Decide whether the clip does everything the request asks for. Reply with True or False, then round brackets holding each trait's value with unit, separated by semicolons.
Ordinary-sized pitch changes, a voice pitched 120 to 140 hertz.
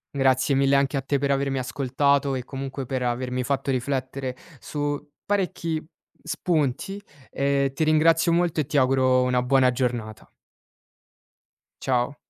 False (2.1 semitones; 135 Hz)